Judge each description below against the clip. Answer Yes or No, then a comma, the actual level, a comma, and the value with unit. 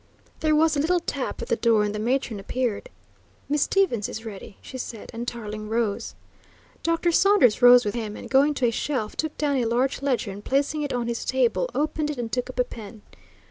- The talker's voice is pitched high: Yes, high, 245 Hz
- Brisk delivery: Yes, fast, 220 wpm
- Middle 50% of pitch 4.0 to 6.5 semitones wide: Yes, average, 4.6 semitones